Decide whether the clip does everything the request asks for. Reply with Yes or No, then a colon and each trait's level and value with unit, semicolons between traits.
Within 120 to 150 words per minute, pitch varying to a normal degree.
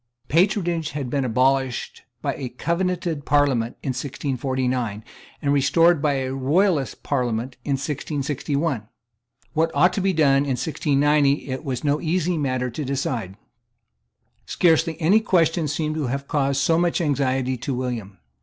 Yes: average, 145 wpm; average, 3.7 semitones